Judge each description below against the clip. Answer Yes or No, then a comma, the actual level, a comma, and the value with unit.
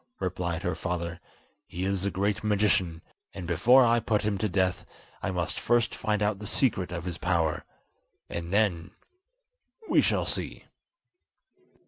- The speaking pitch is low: Yes, very low, 95 Hz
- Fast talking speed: No, average, 145 wpm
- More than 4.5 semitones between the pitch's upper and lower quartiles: No, average, 3.8 semitones